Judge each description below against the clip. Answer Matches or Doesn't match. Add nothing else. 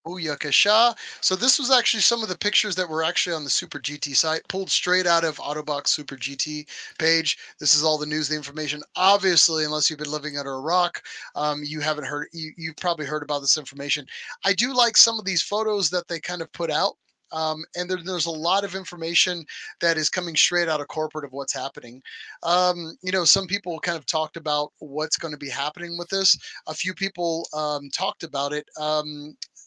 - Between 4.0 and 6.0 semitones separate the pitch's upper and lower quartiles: Doesn't match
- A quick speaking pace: Matches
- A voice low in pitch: Doesn't match